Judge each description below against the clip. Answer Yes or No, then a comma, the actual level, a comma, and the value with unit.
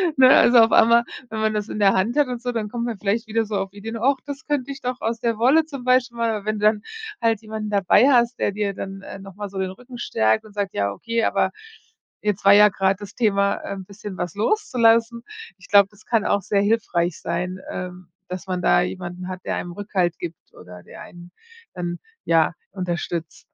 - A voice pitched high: Yes, high, 205 Hz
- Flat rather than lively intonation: No, average, 3.8 semitones